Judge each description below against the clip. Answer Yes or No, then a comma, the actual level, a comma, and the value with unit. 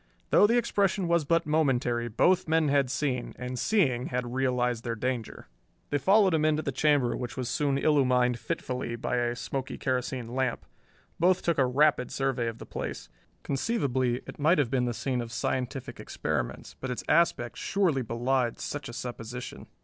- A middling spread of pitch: Yes, average, 3.7 semitones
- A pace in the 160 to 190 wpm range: Yes, average, 175 wpm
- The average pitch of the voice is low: Yes, low, 130 Hz